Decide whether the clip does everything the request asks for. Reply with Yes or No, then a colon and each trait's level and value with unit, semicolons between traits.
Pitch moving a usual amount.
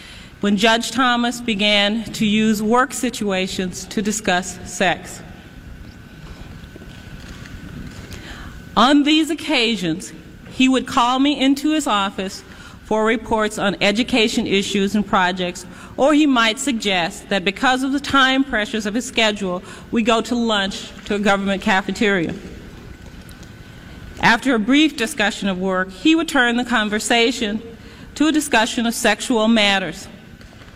Yes: average, 3.8 semitones